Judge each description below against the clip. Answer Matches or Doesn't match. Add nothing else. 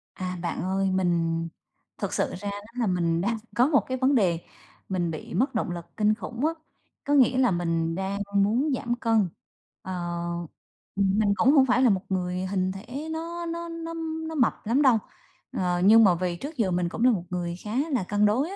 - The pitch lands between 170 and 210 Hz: Matches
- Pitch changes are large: Matches